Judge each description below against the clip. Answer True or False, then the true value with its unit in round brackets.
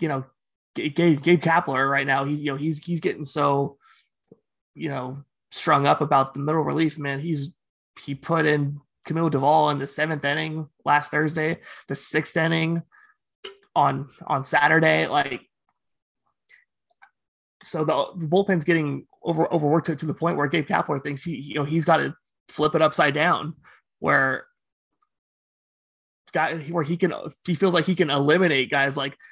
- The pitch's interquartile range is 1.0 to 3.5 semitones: True (2.8 semitones)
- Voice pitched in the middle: True (155 Hz)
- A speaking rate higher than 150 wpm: True (165 wpm)